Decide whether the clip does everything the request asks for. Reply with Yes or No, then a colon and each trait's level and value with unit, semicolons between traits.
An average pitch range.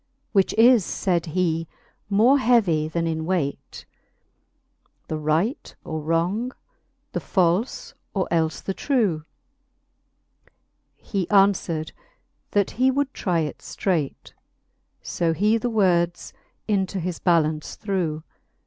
Yes: average, 4.4 semitones